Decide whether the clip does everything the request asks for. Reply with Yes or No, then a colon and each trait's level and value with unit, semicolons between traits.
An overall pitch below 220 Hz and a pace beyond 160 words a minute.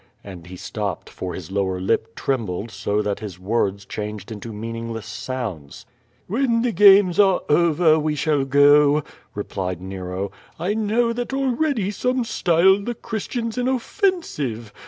No: medium, 140 Hz; average, 140 wpm